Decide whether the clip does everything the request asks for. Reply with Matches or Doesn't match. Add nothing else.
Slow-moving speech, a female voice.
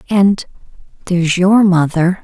Matches